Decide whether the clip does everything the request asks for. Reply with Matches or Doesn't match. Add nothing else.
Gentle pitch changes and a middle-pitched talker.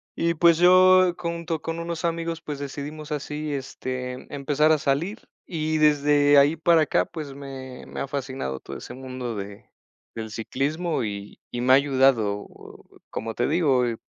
Doesn't match